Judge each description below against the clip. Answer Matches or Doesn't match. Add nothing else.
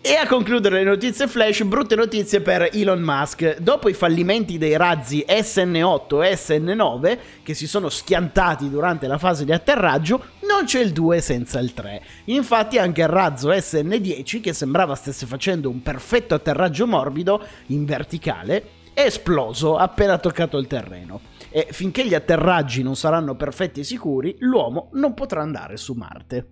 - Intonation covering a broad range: Matches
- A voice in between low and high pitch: Matches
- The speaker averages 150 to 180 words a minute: Matches